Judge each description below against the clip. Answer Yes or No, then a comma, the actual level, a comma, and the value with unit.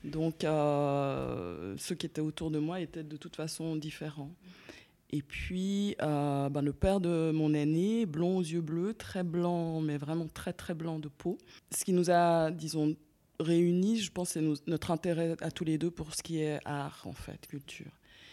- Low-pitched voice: No, medium, 160 Hz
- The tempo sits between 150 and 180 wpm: No, average, 195 wpm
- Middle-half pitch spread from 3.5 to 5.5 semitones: No, narrow, 2.4 semitones